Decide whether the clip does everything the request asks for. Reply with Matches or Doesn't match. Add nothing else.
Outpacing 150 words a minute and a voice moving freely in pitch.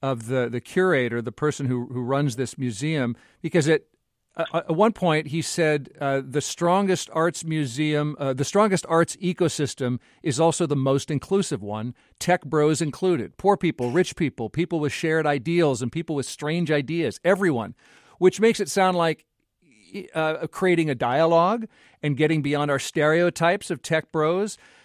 Doesn't match